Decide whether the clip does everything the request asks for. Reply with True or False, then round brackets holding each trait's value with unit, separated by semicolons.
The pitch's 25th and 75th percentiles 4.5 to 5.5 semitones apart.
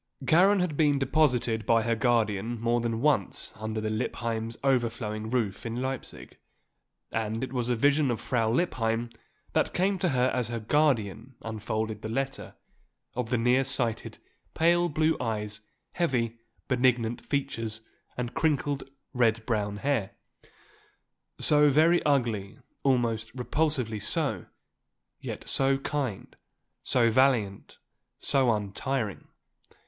False (3.6 semitones)